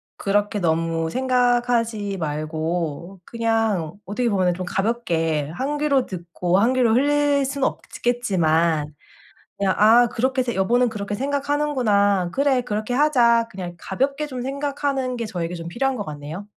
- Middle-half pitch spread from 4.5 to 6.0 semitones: No, wide, 6.4 semitones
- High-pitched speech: Yes, high, 220 Hz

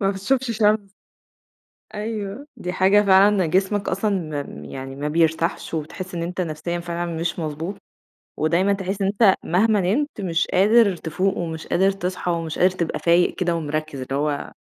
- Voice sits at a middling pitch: Yes, medium, 180 Hz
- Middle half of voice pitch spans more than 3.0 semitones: Yes, average, 3.4 semitones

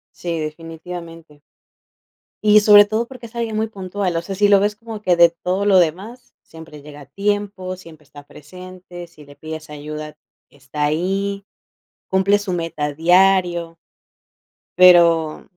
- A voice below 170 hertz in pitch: No, medium, 180 Hz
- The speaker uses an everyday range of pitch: Yes, average, 4.1 semitones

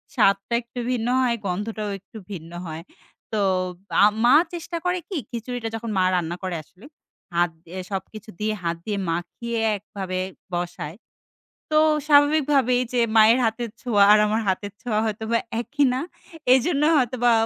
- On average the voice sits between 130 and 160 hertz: No, high, 220 Hz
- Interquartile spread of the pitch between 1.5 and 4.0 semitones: No, average, 4.4 semitones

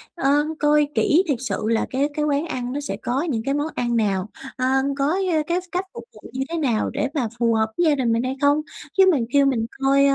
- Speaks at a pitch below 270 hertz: No, very high, 275 Hz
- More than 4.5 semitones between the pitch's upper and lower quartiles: No, average, 3.8 semitones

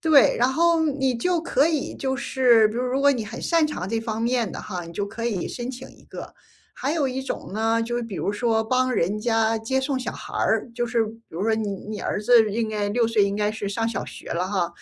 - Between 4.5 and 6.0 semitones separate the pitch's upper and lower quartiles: No, average, 3.5 semitones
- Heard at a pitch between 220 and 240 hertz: Yes, high, 230 Hz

